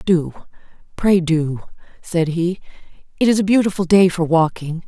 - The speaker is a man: No, female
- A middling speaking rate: Yes, average, 150 wpm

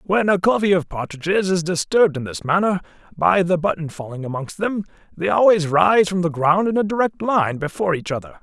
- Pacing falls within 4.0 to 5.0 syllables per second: No, 5.6 syllables/s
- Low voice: No, medium, 175 Hz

